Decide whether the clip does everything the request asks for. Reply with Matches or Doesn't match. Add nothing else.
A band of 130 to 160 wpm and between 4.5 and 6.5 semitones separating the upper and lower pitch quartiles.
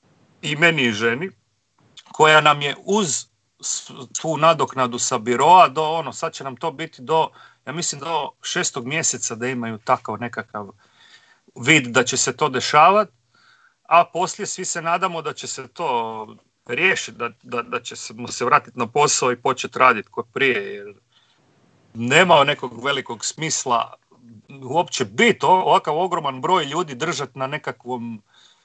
Matches